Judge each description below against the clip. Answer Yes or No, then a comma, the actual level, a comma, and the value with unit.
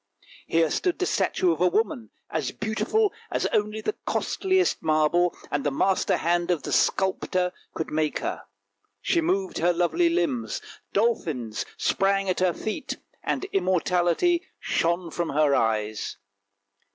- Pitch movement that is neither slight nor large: No, wide, 6.9 semitones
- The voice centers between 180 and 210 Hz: Yes, medium, 185 Hz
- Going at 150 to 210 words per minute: No, average, 140 wpm